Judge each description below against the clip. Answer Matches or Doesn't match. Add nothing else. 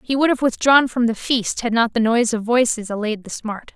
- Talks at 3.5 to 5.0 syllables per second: Doesn't match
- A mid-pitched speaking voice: Doesn't match